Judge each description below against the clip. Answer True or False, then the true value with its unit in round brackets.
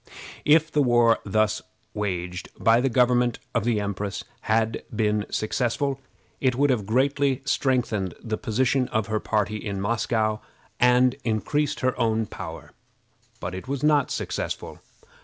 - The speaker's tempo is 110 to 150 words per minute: True (140 wpm)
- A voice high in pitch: False (115 Hz)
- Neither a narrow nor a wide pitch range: True (3.3 semitones)